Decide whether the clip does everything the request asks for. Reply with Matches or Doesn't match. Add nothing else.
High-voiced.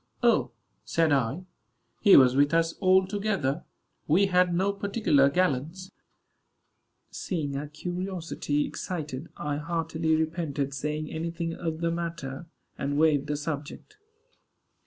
Doesn't match